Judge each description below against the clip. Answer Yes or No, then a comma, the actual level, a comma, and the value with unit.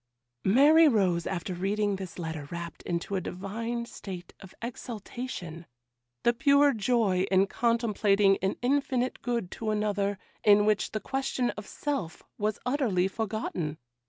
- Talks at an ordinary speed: No, slow, 130 wpm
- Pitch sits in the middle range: No, high, 205 Hz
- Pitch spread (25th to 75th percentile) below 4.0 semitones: No, average, 4.5 semitones